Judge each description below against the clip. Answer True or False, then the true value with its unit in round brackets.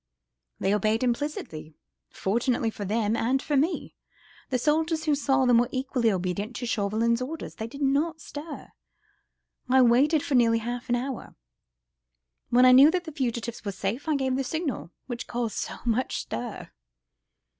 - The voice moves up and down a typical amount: True (3.7 semitones)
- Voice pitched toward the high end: True (245 Hz)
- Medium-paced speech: True (165 wpm)